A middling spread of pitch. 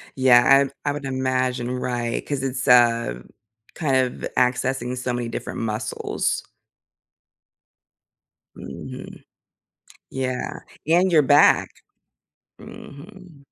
No: narrow, 2.3 semitones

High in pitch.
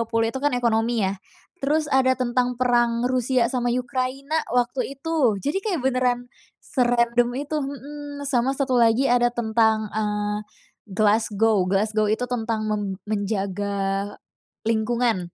Yes: high, 240 Hz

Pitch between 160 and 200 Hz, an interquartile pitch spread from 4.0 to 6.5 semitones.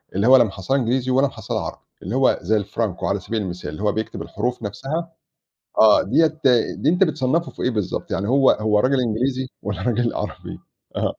No: low, 120 Hz; average, 4.3 semitones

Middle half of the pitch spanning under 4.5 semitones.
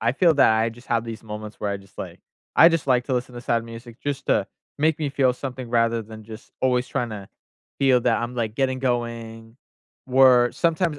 Yes: average, 2.7 semitones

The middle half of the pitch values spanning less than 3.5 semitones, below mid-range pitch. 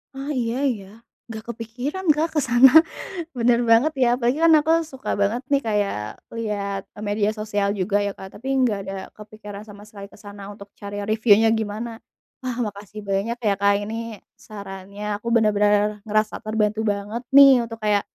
No: average, 2.7 semitones; high, 215 Hz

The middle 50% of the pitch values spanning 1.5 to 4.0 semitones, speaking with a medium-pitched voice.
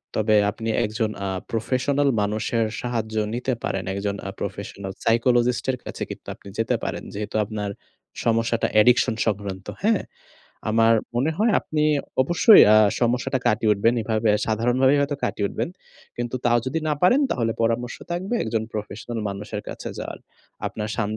No: average, 2.9 semitones; low, 115 Hz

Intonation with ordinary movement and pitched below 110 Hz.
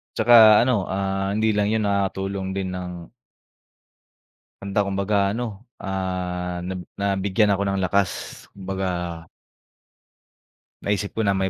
No: narrow, 1.4 semitones; low, 100 Hz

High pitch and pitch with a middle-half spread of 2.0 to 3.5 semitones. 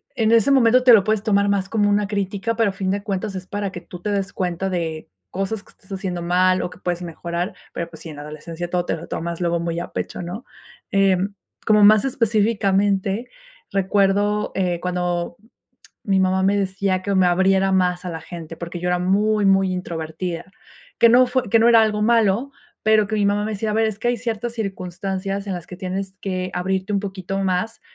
Yes: high, 195 Hz; average, 2.7 semitones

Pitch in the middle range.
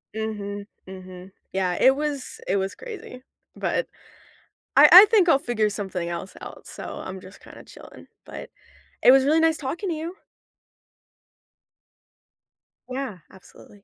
No: high, 220 Hz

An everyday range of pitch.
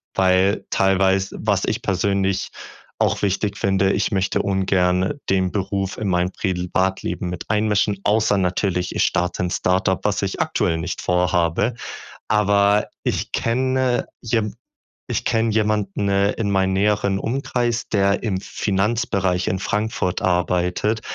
No: narrow, 2.1 semitones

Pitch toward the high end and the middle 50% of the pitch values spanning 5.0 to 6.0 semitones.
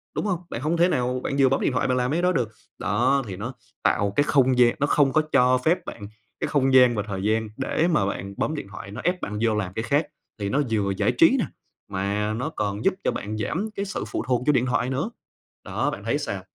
No: low, 125 Hz; average, 5.3 semitones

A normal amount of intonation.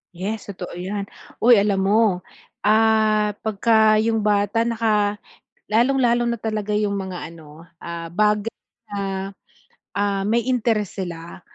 No: narrow, 2.2 semitones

